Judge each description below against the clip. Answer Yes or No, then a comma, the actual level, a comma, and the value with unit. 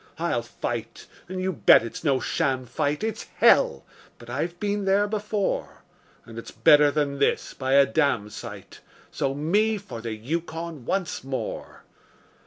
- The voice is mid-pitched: Yes, medium, 145 Hz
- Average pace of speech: Yes, average, 150 wpm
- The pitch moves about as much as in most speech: No, wide, 6.5 semitones